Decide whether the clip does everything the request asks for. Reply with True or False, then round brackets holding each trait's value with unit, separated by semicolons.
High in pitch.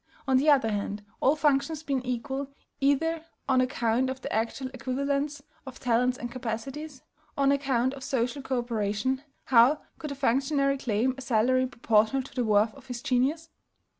True (260 Hz)